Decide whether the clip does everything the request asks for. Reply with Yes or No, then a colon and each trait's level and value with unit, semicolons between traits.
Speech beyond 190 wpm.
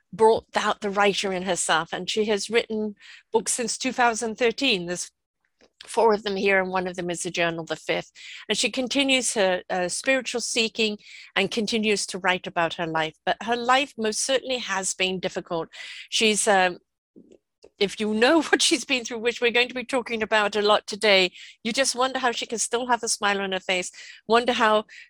Yes: average, 200 wpm